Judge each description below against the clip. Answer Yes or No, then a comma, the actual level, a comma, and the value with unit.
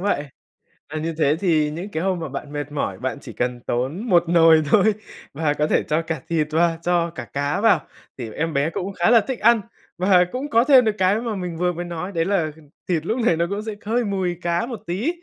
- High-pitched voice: No, medium, 170 Hz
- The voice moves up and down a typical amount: Yes, average, 4.5 semitones